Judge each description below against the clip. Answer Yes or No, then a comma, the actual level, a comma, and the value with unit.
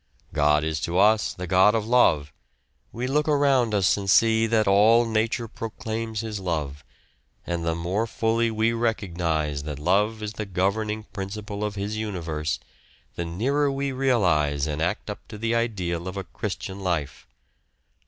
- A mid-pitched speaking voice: No, low, 105 Hz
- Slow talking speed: No, average, 165 wpm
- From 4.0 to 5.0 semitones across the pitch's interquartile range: Yes, average, 4.7 semitones